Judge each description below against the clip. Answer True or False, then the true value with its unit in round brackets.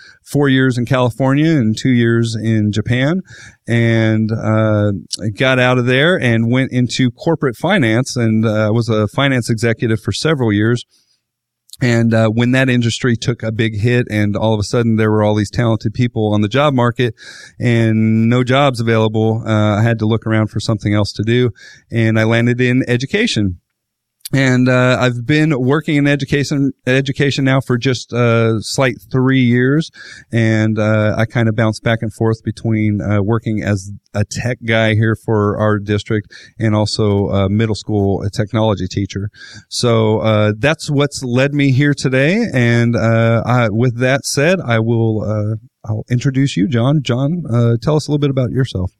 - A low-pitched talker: True (115 Hz)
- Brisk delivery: False (180 wpm)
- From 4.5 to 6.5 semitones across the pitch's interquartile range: False (2.9 semitones)